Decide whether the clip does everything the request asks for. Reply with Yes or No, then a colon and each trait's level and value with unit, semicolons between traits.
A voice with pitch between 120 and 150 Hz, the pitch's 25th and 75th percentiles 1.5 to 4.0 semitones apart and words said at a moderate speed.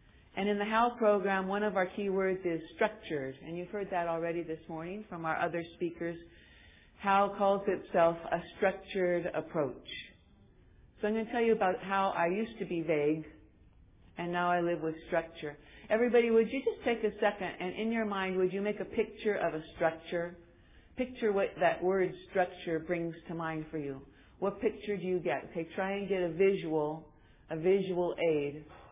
No: medium, 175 Hz; average, 3.5 semitones; average, 190 wpm